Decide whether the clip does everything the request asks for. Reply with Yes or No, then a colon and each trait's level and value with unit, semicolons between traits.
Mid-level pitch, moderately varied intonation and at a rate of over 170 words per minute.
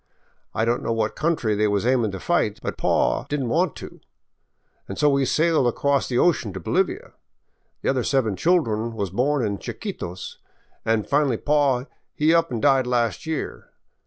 No: low, 125 Hz; average, 4.9 semitones; average, 185 wpm